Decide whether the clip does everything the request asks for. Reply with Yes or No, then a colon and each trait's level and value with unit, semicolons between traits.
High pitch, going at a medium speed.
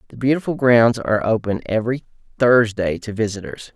No: low, 115 Hz; average, 145 wpm